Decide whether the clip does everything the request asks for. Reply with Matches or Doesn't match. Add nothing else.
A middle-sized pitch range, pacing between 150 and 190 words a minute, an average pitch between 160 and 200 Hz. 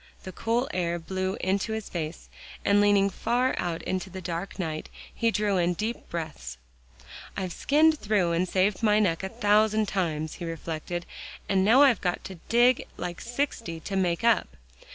Matches